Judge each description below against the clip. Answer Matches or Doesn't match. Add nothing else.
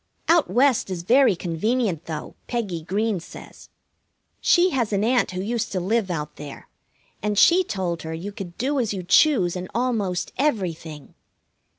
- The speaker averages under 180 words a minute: Matches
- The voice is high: Matches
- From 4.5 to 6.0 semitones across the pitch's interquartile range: Matches